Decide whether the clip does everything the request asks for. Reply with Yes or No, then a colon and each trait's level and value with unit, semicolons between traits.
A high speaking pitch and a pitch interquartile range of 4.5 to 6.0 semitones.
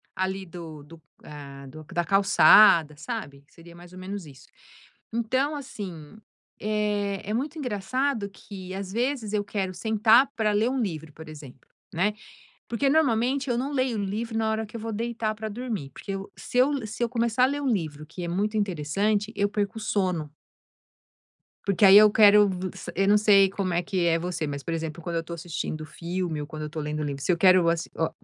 Yes: high, 195 Hz; average, 4.8 semitones